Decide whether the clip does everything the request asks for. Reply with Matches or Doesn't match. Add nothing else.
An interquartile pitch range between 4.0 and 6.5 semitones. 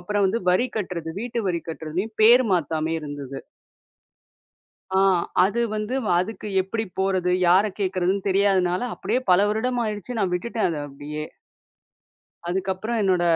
Doesn't match